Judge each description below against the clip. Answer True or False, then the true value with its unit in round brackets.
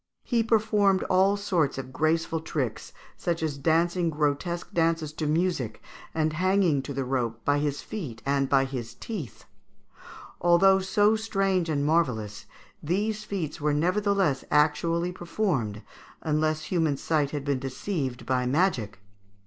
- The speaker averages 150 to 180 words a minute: False (140 wpm)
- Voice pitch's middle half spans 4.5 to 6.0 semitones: True (5.1 semitones)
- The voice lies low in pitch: False (160 Hz)